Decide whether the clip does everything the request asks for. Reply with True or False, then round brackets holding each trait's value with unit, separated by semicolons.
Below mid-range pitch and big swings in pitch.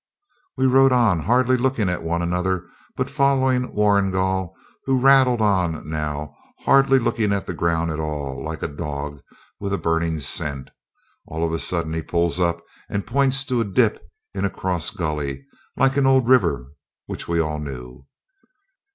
True (90 Hz; 7.7 semitones)